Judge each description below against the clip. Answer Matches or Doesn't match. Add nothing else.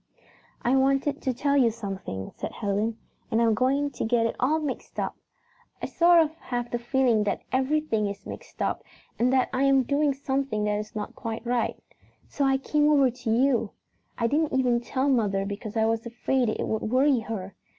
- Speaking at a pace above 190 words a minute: Matches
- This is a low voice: Doesn't match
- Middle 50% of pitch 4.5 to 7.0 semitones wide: Doesn't match